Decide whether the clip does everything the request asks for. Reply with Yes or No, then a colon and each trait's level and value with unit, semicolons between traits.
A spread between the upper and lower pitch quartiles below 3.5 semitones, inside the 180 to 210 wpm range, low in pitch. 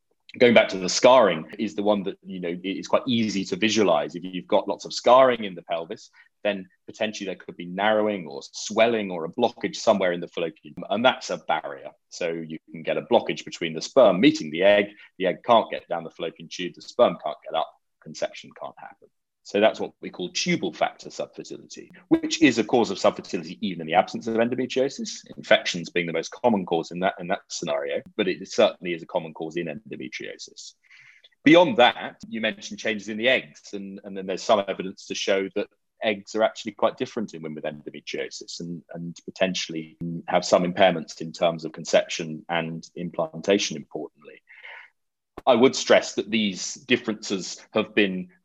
No: average, 4.4 semitones; average, 200 wpm; very low, 95 Hz